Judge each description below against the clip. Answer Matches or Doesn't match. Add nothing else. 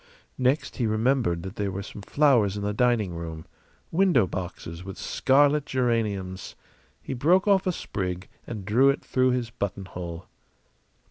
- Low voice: Matches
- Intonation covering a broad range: Matches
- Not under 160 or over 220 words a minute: Doesn't match